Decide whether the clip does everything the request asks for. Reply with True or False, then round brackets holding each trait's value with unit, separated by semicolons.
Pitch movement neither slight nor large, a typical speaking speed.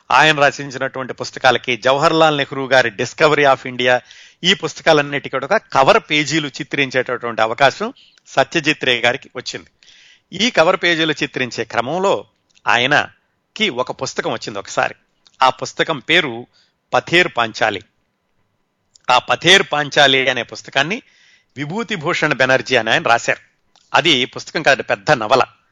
True (4.0 semitones; 115 wpm)